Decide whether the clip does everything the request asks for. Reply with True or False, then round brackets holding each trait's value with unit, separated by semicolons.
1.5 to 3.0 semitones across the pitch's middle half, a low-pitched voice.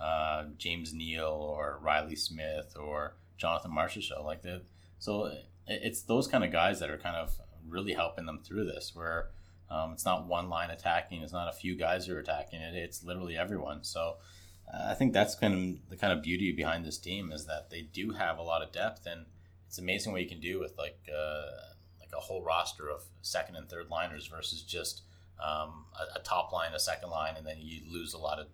True (2.4 semitones; 85 Hz)